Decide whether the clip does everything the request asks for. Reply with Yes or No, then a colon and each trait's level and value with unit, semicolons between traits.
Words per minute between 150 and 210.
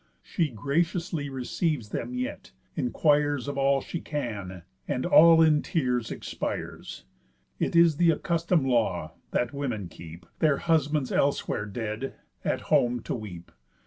No: slow, 135 wpm